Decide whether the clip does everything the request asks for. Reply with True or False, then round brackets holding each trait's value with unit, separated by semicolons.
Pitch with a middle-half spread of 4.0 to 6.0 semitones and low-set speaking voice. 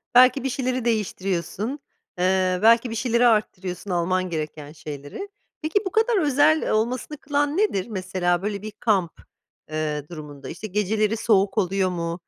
False (5.5 semitones; 200 Hz)